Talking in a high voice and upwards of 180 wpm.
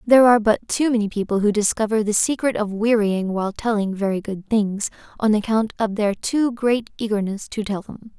Yes: high, 215 Hz; average, 200 wpm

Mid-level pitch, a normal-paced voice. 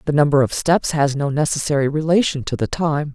No: medium, 145 Hz; fast, 210 wpm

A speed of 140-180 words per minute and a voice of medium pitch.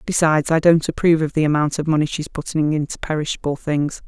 No: fast, 205 wpm; medium, 155 Hz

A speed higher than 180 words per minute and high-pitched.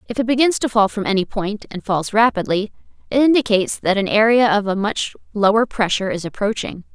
Yes: average, 200 wpm; high, 210 Hz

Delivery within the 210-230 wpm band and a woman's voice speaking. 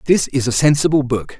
No: fast, 215 wpm; male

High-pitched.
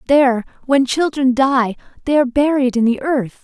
Yes: very high, 265 Hz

